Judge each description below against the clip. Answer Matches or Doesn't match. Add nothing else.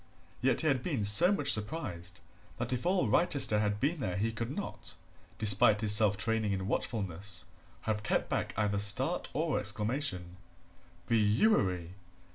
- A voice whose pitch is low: Matches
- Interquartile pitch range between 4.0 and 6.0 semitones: Matches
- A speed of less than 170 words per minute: Matches